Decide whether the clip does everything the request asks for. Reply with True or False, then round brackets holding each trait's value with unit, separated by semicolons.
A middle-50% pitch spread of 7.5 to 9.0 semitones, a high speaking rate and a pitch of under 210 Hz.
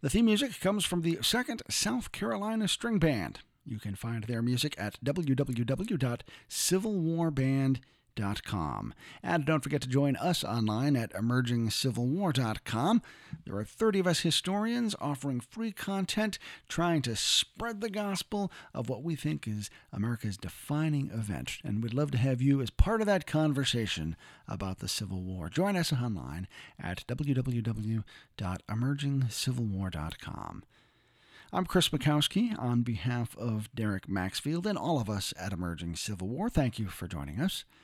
False (7.8 semitones; 145 wpm; 135 Hz)